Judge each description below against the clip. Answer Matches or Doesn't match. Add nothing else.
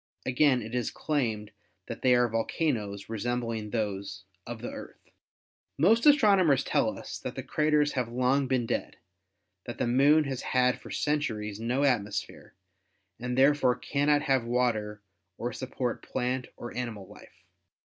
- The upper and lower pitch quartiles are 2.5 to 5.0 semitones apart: Matches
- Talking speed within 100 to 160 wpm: Matches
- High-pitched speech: Doesn't match